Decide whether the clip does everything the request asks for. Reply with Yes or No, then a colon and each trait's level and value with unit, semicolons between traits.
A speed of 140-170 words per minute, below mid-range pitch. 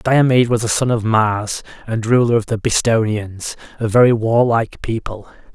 Yes: average, 160 wpm; low, 115 Hz